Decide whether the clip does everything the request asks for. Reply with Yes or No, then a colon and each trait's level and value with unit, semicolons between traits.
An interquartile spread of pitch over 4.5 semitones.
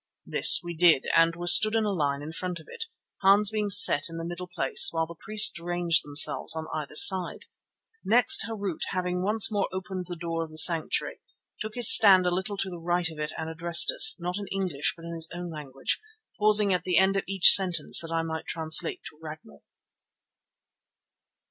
No: average, 3.2 semitones